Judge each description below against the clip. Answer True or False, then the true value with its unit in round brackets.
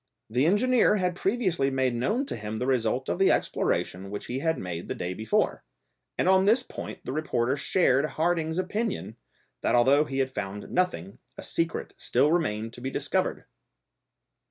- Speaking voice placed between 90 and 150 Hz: True (135 Hz)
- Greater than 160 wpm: True (175 wpm)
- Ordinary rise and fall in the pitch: False (7.5 semitones)